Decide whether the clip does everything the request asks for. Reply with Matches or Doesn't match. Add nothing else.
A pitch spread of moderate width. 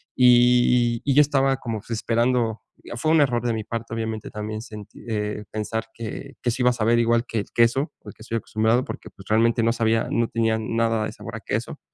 Doesn't match